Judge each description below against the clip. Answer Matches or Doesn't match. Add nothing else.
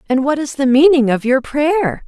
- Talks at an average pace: Doesn't match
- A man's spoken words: Doesn't match